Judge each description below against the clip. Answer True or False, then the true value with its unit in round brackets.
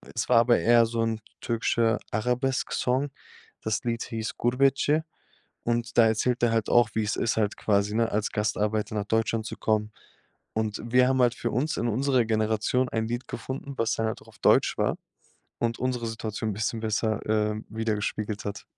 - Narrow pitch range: True (1.8 semitones)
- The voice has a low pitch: True (115 Hz)